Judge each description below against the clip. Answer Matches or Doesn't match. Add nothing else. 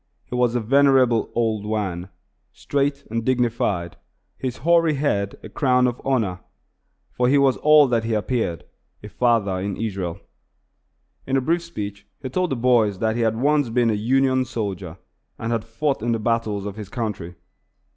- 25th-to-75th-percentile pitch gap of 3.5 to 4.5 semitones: Matches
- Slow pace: Doesn't match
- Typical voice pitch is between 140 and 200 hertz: Doesn't match